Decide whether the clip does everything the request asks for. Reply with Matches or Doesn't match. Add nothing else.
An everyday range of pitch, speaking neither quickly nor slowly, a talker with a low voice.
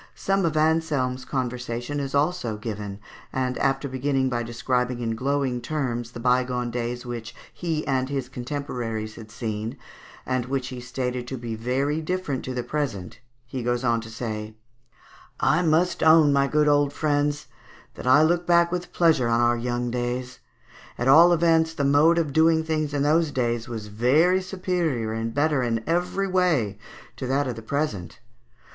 Matches